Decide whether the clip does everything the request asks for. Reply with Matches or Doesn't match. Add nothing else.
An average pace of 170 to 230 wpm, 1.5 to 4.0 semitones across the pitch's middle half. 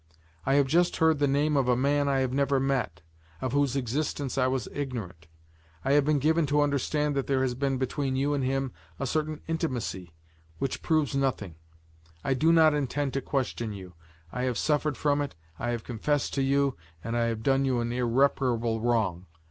Matches